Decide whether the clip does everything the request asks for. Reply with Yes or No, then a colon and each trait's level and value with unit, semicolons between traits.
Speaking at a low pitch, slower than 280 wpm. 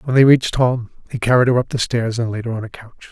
No: low, 120 Hz; fast, 310 wpm